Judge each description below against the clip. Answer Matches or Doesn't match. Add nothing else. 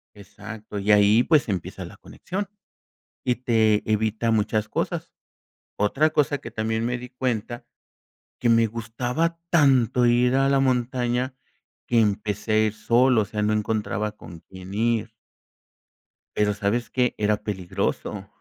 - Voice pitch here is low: Matches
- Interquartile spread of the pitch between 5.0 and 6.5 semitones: Doesn't match